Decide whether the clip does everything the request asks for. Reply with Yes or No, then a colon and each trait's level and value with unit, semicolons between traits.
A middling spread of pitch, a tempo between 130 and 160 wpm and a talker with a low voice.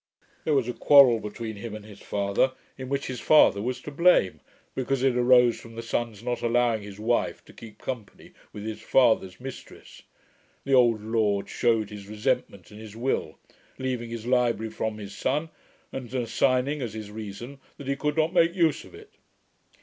No: average, 3.5 semitones; average, 185 wpm; low, 120 Hz